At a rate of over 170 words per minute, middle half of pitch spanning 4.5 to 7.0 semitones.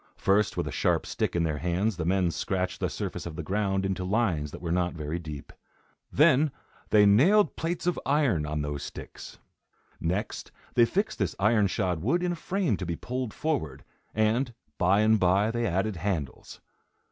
Yes: average, 185 wpm; wide, 5.4 semitones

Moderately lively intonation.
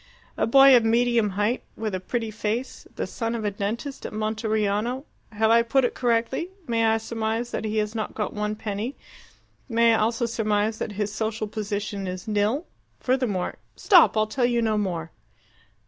No: narrow, 2.0 semitones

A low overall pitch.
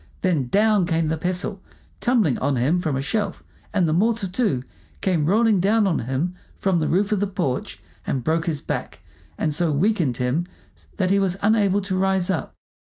No: medium, 180 Hz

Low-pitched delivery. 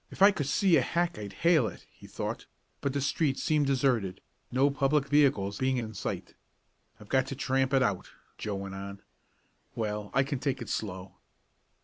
Yes: low, 130 Hz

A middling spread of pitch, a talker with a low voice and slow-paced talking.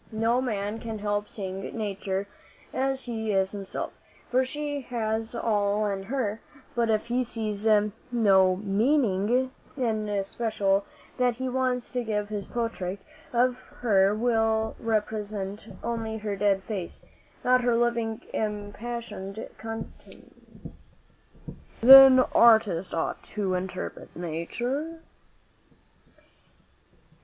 No: average, 3.0 semitones; high, 220 Hz; slow, 110 wpm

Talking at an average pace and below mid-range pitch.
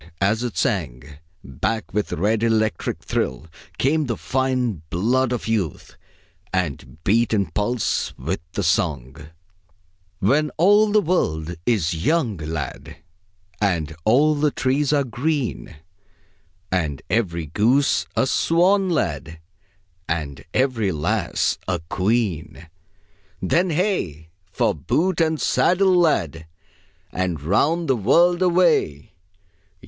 No: slow, 115 wpm; low, 110 Hz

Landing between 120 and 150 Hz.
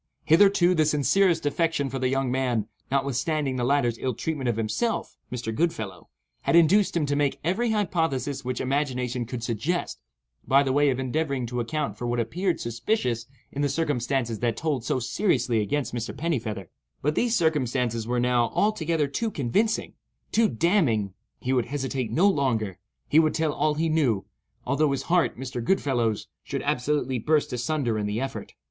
Yes: low, 135 Hz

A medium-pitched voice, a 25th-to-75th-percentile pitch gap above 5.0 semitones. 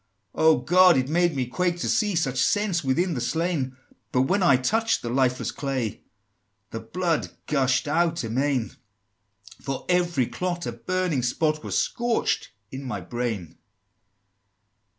Yes: medium, 145 Hz; wide, 5.6 semitones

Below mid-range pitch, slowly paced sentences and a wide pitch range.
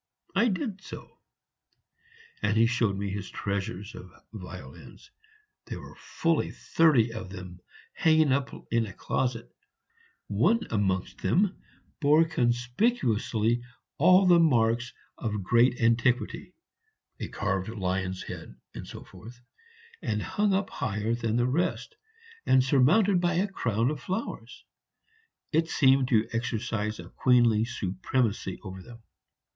Yes: low, 120 Hz; slow, 125 wpm; wide, 6.4 semitones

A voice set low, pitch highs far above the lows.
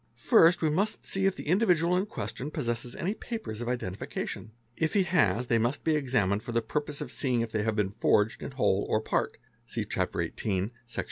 Yes: low, 125 Hz; wide, 7.2 semitones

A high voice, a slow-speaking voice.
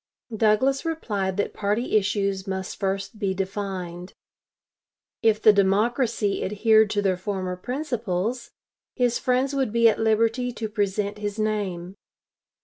Yes: high, 210 Hz; slow, 130 wpm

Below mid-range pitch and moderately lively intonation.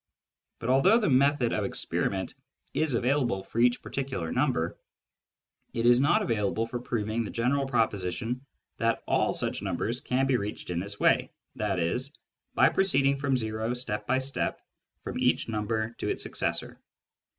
Yes: low, 120 Hz; average, 3.8 semitones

